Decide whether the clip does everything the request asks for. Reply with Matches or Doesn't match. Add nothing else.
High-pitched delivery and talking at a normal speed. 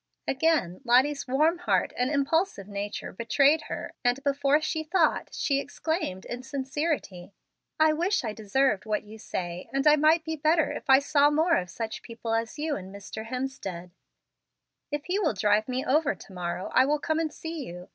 Matches